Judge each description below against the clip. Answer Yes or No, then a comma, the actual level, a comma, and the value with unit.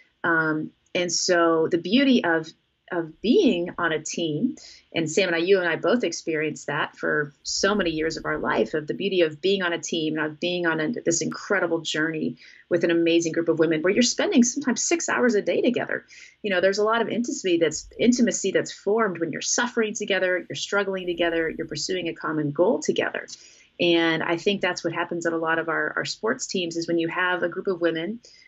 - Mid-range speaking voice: Yes, medium, 175 Hz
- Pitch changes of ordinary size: Yes, average, 3.3 semitones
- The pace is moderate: No, fast, 220 wpm